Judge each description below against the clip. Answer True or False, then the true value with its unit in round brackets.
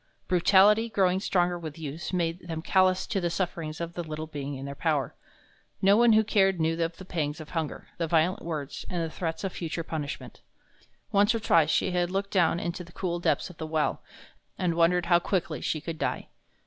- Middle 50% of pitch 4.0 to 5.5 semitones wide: False (2.7 semitones)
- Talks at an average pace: False (210 wpm)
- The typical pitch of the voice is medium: True (170 Hz)